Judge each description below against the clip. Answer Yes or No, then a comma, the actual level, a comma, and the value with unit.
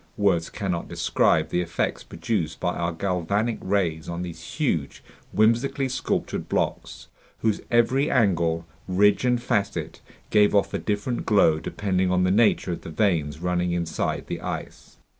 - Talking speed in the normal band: Yes, average, 150 wpm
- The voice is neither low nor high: No, very low, 95 Hz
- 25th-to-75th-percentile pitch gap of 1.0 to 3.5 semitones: No, average, 3.9 semitones